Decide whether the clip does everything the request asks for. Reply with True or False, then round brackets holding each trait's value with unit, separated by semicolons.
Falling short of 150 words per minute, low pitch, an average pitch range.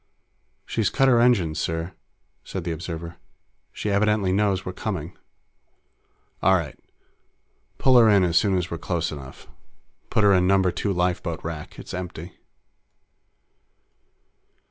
True (135 wpm; 90 Hz; 3.3 semitones)